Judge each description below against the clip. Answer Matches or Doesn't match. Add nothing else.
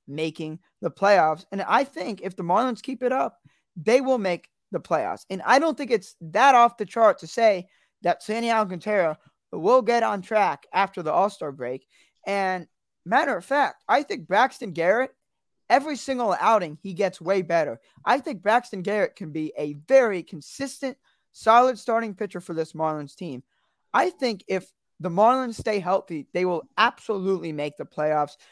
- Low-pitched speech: Doesn't match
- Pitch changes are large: Matches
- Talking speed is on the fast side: Doesn't match